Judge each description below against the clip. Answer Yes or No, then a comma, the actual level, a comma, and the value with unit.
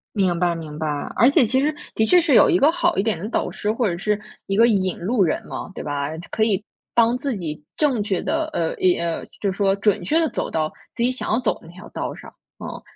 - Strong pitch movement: Yes, wide, 6.1 semitones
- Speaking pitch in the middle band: No, high, 210 Hz